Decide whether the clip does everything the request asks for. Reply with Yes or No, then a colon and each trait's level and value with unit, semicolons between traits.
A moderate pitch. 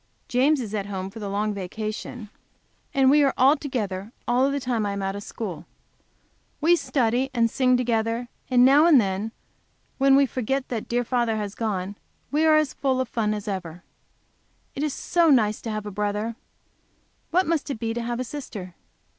No: high, 235 Hz